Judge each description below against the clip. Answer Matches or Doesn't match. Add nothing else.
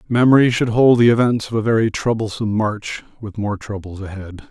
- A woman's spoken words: Doesn't match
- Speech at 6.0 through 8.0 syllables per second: Doesn't match